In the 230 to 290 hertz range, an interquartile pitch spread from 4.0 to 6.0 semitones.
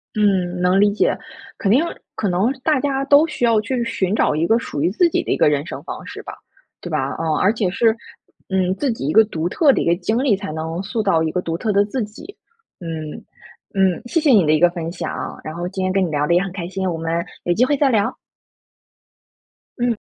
No: high, 195 Hz; average, 5.2 semitones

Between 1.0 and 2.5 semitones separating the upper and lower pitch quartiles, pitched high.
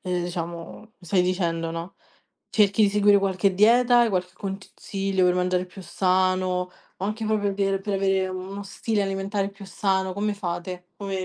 Yes: narrow, 1.8 semitones; high, 195 Hz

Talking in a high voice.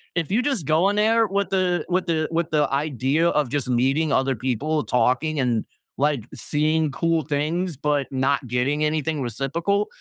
No: medium, 150 Hz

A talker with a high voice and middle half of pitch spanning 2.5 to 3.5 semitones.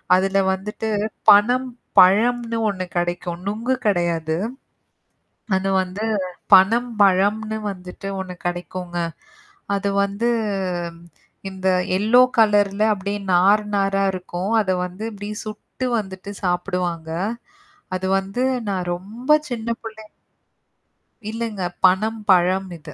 Yes: high, 195 Hz; average, 2.9 semitones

